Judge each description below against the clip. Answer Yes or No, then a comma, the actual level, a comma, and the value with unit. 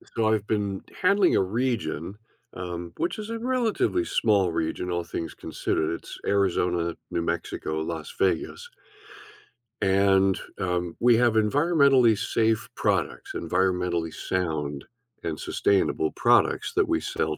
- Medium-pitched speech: No, very low, 95 Hz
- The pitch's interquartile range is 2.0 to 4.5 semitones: No, wide, 5.5 semitones